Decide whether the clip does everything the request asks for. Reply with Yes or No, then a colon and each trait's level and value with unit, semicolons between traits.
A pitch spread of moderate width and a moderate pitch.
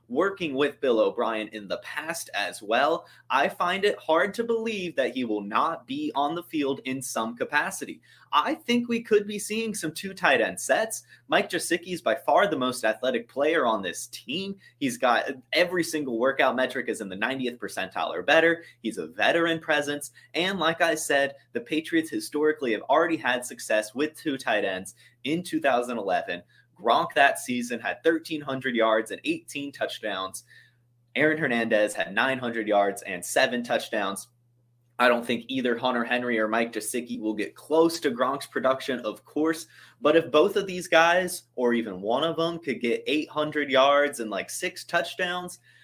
No: wide, 6.1 semitones; medium, 150 Hz